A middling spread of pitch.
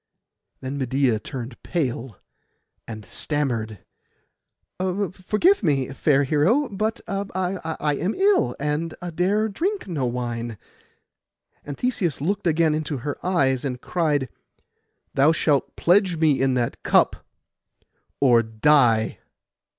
No: wide, 6.2 semitones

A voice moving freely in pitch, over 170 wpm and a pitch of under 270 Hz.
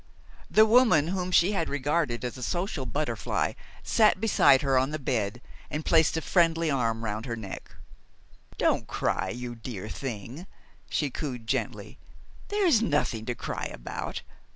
No: wide, 6.2 semitones; average, 155 wpm; medium, 140 Hz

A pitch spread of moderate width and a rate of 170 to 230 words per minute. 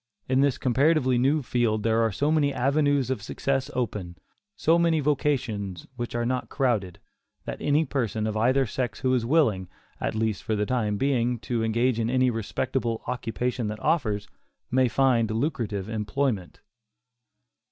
No: average, 3.6 semitones; average, 160 wpm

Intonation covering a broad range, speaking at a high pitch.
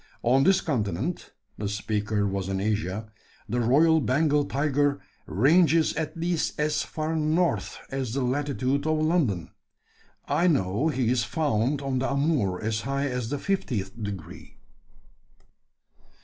No: wide, 6.0 semitones; low, 135 Hz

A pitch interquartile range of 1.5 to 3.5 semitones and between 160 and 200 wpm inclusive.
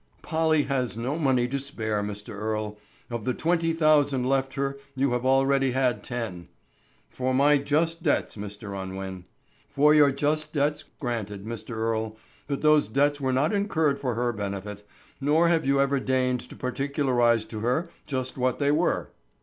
No: average, 4.3 semitones; average, 165 wpm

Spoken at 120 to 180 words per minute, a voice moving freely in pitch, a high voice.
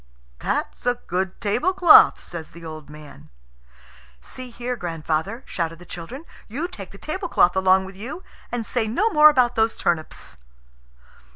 Yes: average, 150 wpm; wide, 7.0 semitones; high, 205 Hz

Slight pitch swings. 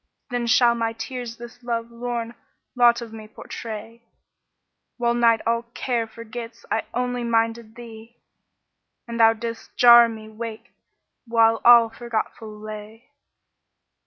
Yes: narrow, 1.0 semitones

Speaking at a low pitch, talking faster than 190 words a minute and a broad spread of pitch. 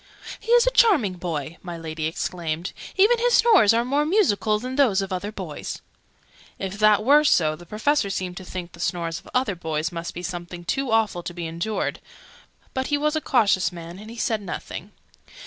No: high, 200 Hz; average, 200 wpm; wide, 7.2 semitones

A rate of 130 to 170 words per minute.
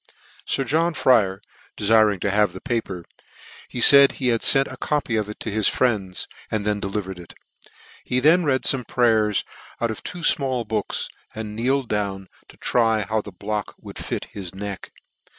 No: average, 180 wpm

